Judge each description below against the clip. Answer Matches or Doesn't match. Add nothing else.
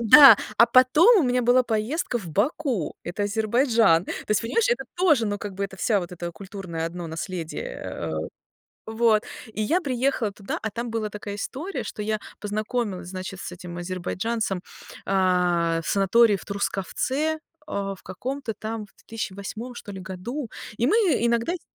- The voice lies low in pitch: Doesn't match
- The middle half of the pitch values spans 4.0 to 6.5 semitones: Matches